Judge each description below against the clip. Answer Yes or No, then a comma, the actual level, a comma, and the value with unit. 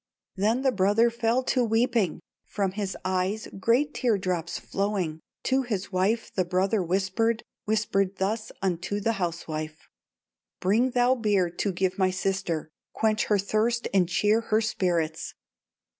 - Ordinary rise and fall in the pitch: Yes, average, 3.6 semitones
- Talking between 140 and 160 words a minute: Yes, average, 145 wpm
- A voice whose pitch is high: Yes, high, 200 Hz